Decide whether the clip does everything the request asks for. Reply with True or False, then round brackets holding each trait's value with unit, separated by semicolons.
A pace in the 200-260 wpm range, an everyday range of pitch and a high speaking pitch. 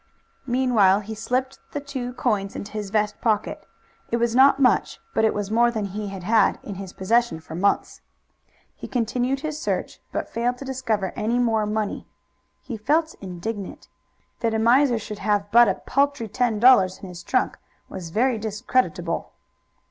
False (170 wpm; 3.5 semitones; 220 Hz)